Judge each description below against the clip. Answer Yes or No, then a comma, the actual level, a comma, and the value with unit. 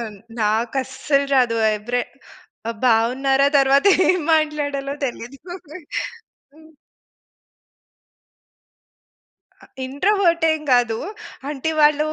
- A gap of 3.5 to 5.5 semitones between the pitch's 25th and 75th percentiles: Yes, average, 4.1 semitones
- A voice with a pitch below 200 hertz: No, very high, 275 Hz